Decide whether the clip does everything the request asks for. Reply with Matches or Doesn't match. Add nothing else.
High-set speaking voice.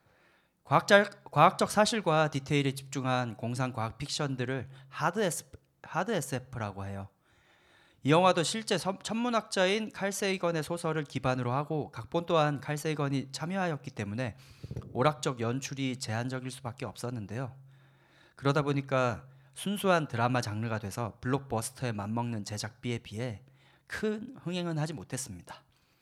Doesn't match